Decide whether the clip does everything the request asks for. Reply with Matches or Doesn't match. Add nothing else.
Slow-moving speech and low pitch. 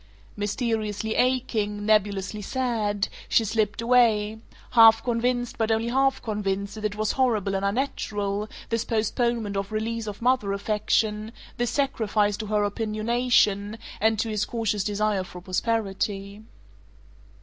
Doesn't match